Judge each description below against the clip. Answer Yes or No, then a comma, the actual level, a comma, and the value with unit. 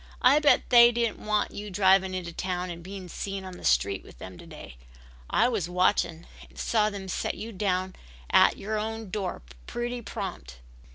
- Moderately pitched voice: No, high, 195 Hz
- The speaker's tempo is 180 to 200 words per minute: Yes, average, 185 wpm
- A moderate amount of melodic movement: Yes, average, 3.2 semitones